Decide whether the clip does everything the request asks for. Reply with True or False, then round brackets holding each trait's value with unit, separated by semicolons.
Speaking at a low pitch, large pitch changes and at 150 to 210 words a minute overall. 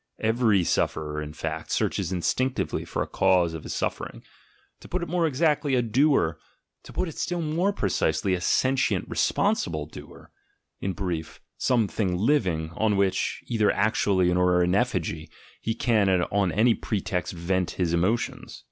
True (100 Hz; 5.7 semitones; 160 wpm)